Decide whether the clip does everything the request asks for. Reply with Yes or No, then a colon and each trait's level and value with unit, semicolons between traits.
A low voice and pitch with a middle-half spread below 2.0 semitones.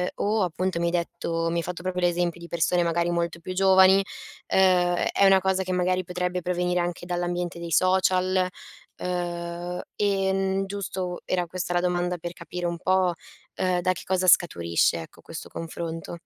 No: medium, 180 Hz; narrow, 1.3 semitones